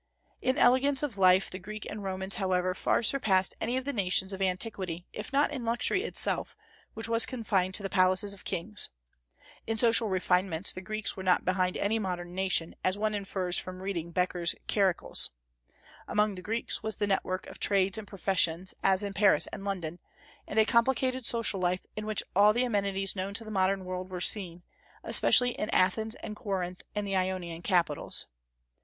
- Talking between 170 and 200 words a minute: Yes, average, 185 wpm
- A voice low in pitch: No, high, 195 Hz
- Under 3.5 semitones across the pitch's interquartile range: Yes, average, 2.8 semitones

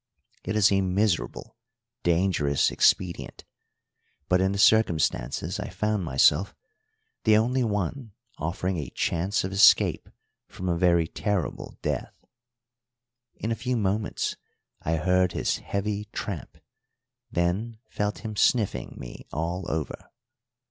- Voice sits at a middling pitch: No, very low, 95 Hz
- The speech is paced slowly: Yes, slow, 120 wpm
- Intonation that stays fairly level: No, average, 3.6 semitones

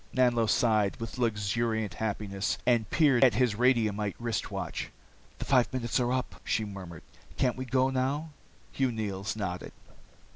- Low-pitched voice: Yes, low, 115 Hz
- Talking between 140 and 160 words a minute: Yes, average, 150 wpm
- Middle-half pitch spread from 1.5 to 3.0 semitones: No, average, 3.5 semitones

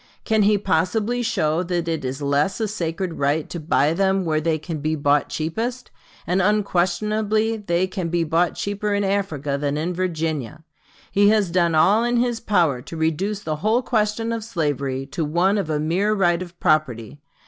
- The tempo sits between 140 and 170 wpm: No, average, 185 wpm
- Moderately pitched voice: Yes, medium, 175 Hz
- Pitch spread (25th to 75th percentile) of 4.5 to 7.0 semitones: Yes, average, 5.0 semitones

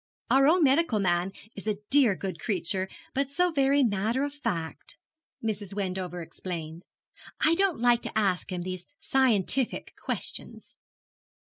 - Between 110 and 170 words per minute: Yes, average, 140 wpm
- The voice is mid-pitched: No, high, 215 Hz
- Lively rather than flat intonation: Yes, wide, 6.8 semitones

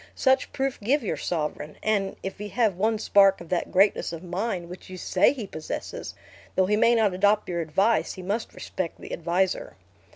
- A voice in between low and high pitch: No, high, 195 Hz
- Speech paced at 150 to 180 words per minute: No, average, 195 wpm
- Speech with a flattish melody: No, average, 3.3 semitones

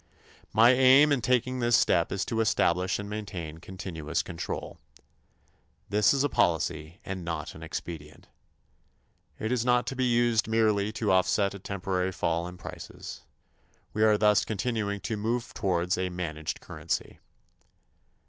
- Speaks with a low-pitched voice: Yes, low, 100 Hz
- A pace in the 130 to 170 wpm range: Yes, average, 150 wpm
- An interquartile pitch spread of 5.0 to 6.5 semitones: No, average, 4.4 semitones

